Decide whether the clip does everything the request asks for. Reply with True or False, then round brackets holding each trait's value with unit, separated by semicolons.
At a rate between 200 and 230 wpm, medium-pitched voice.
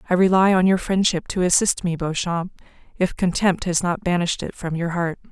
True (205 wpm; 180 Hz)